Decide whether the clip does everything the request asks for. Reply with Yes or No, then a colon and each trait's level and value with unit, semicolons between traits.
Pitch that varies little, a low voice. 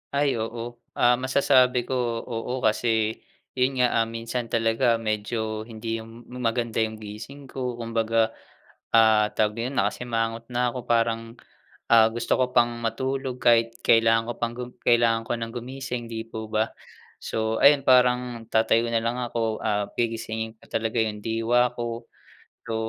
Yes: narrow, 1.5 semitones; low, 115 Hz